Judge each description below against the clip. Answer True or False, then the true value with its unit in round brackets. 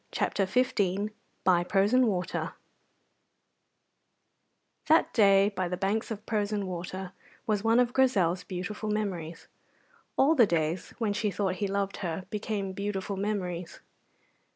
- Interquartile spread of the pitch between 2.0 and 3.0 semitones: True (2.7 semitones)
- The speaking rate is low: True (130 wpm)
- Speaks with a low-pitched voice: False (200 Hz)